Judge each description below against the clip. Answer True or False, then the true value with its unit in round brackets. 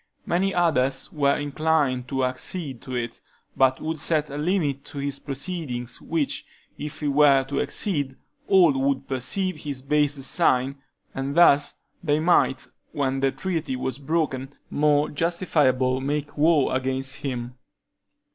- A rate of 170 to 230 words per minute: False (140 wpm)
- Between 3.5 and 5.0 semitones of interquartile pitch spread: False (2.9 semitones)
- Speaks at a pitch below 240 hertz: True (140 Hz)